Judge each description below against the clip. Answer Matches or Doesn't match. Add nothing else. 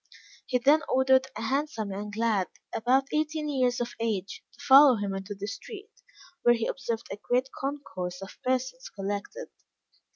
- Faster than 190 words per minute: Doesn't match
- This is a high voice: Matches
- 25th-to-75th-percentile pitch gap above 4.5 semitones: Matches